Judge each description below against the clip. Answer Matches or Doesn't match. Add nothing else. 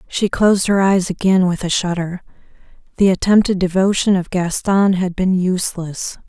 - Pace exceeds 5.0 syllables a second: Doesn't match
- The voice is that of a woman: Matches